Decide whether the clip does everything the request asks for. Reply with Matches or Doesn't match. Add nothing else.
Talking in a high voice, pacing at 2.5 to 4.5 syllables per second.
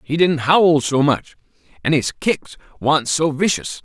Doesn't match